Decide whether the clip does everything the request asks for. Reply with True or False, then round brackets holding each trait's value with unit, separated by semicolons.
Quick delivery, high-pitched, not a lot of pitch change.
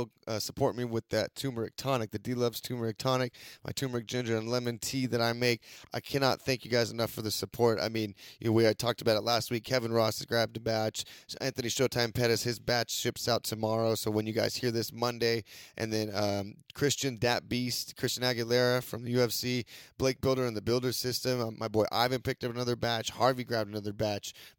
False (220 wpm; 120 Hz; 2.0 semitones)